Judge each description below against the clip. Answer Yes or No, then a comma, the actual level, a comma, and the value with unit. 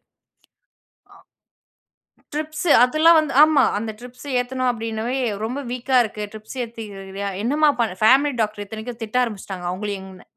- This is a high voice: Yes, high, 235 Hz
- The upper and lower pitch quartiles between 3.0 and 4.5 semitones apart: Yes, average, 3.9 semitones